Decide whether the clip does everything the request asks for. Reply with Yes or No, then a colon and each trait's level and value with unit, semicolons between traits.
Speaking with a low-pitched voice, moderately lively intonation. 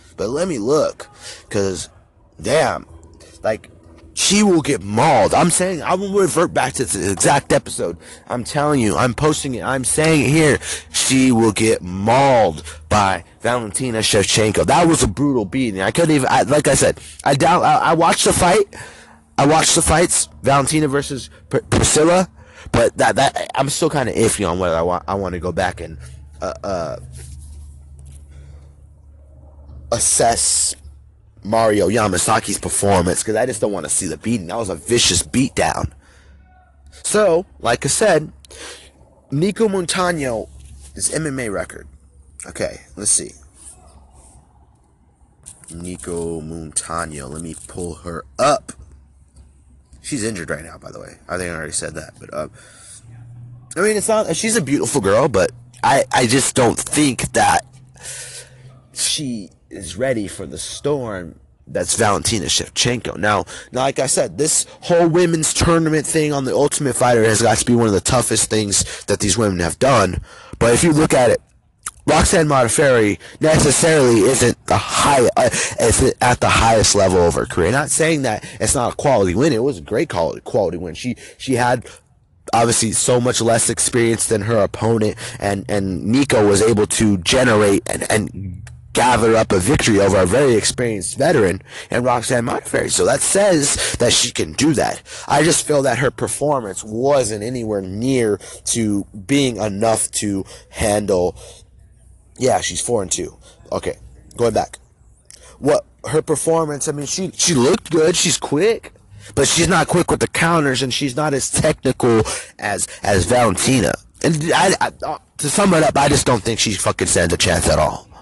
No: low, 110 Hz; wide, 8.2 semitones